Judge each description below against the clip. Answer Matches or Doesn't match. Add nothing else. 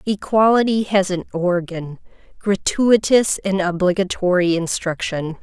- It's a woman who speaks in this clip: Matches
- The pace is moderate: Doesn't match